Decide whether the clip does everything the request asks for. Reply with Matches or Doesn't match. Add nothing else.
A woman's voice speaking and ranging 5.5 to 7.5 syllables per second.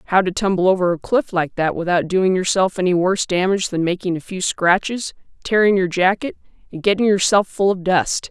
Matches